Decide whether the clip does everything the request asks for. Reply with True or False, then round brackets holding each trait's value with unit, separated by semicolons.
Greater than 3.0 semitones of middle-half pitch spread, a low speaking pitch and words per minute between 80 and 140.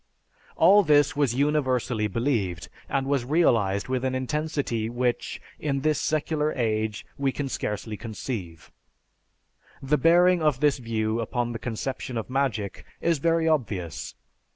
True (4.8 semitones; 130 Hz; 135 wpm)